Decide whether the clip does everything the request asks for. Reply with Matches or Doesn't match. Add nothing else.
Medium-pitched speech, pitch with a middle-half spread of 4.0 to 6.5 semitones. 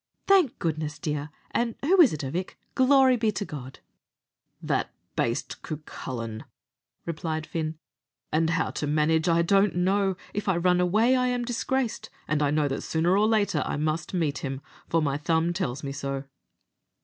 Matches